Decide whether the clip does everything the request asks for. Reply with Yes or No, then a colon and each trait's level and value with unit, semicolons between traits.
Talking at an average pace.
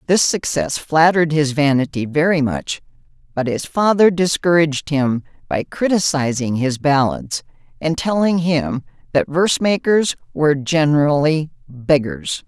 No: slow, 120 wpm